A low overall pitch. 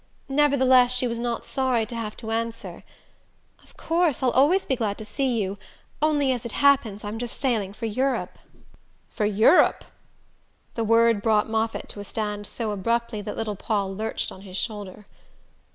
No: high, 230 Hz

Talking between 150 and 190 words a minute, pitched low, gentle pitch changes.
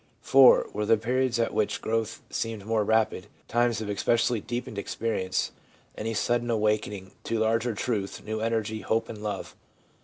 Yes: average, 160 wpm; low, 110 Hz; narrow, 1.6 semitones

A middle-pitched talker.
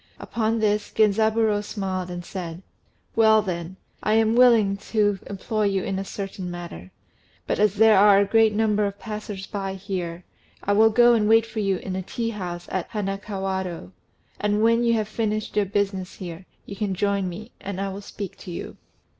No: high, 200 Hz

